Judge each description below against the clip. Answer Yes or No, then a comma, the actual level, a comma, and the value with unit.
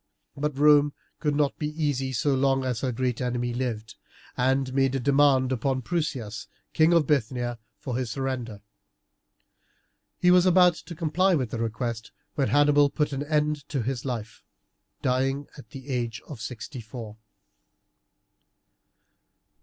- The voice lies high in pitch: No, low, 135 Hz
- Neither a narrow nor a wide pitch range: Yes, average, 3.2 semitones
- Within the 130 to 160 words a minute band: Yes, average, 145 wpm